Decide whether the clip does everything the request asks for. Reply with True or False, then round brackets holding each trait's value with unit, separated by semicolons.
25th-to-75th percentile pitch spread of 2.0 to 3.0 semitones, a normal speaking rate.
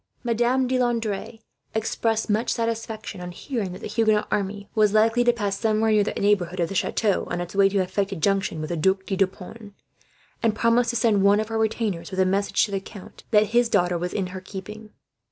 False (2.7 semitones; 225 wpm)